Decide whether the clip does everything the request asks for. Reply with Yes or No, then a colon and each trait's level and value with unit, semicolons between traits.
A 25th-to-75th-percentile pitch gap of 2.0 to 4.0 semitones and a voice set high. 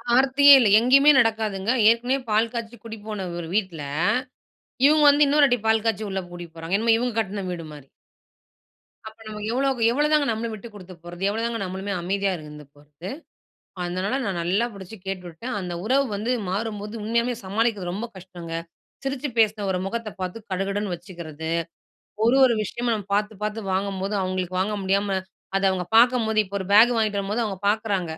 Yes: average, 3.7 semitones; high, 210 Hz